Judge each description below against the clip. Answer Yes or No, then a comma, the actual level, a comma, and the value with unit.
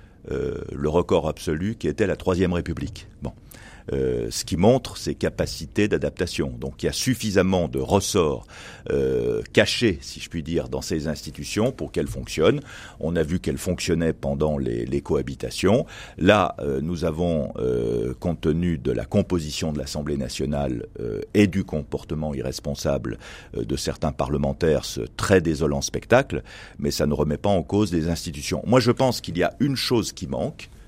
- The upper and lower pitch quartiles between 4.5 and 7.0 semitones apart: Yes, average, 4.8 semitones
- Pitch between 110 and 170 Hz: No, very low, 80 Hz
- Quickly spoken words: No, average, 175 wpm